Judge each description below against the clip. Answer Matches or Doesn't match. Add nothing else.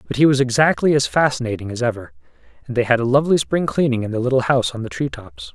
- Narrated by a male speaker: Matches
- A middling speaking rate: Doesn't match